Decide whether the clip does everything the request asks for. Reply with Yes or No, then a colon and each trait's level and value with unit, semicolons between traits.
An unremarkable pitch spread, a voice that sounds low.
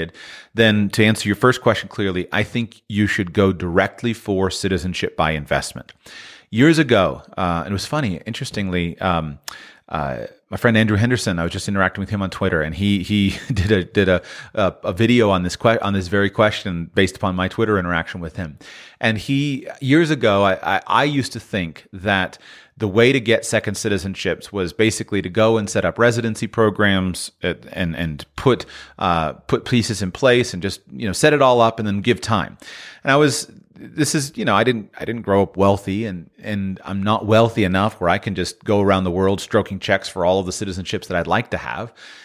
Yes: average, 3.2 semitones; low, 100 Hz